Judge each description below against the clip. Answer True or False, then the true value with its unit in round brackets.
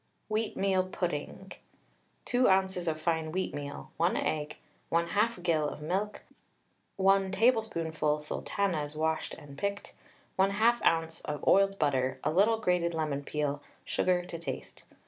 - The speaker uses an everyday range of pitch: True (4.3 semitones)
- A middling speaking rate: False (125 wpm)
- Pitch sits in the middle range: True (170 Hz)